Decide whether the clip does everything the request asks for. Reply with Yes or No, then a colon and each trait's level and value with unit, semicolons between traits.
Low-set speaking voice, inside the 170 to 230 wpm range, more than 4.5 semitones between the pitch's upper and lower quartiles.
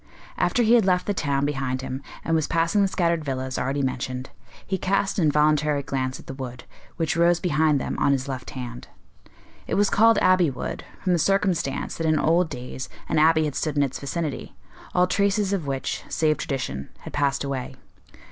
No: medium, 150 Hz; average, 195 wpm; average, 4.9 semitones